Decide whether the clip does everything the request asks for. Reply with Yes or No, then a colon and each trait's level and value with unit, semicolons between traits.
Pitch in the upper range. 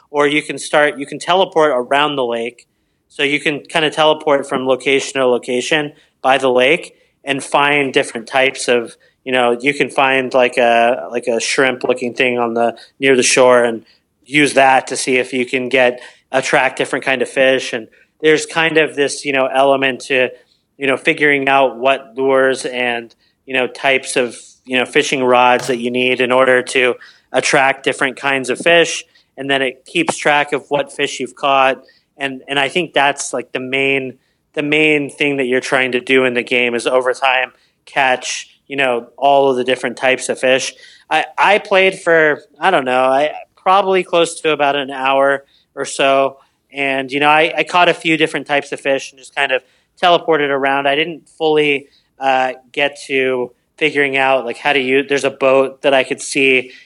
No: low, 135 Hz